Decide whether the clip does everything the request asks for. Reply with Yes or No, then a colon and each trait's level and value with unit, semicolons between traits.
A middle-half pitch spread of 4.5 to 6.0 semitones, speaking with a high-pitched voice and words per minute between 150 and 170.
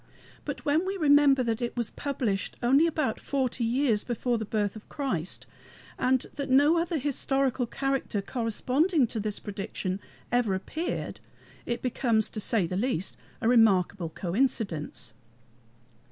No: average, 4.8 semitones; high, 240 Hz; average, 140 wpm